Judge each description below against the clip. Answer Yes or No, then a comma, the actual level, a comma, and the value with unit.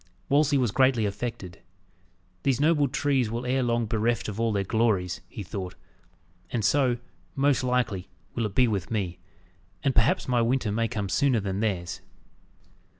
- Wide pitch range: No, average, 3.9 semitones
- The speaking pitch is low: Yes, low, 115 Hz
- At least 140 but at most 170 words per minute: Yes, average, 160 wpm